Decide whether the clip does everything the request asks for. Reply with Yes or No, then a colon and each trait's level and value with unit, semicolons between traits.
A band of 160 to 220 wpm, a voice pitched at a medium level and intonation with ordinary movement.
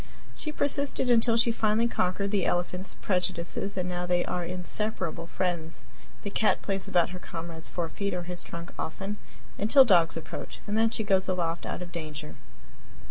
Yes: average, 170 wpm; medium, 180 Hz; average, 3.6 semitones